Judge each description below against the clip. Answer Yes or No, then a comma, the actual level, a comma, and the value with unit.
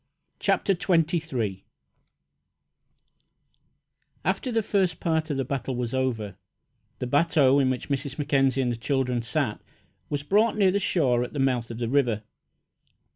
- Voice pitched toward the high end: No, low, 135 Hz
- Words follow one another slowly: No, average, 150 wpm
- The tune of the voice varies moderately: Yes, average, 4.9 semitones